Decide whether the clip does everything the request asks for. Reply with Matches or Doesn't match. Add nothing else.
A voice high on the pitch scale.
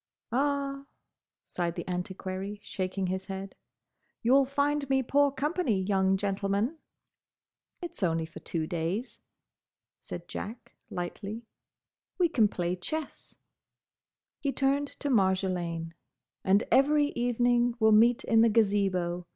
Matches